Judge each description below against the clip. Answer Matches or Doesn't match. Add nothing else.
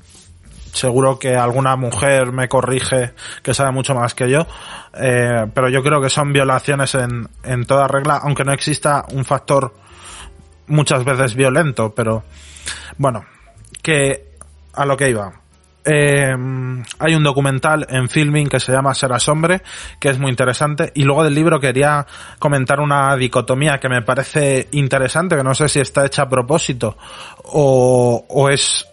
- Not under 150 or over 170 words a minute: Matches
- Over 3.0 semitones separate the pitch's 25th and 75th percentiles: Doesn't match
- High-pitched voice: Doesn't match